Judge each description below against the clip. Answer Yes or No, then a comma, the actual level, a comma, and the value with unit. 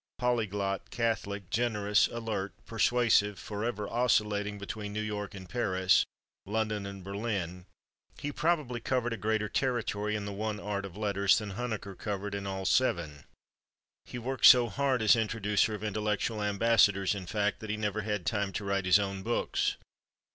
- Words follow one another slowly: No, average, 160 wpm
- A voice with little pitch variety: Yes, narrow, 2.3 semitones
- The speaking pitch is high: No, low, 105 Hz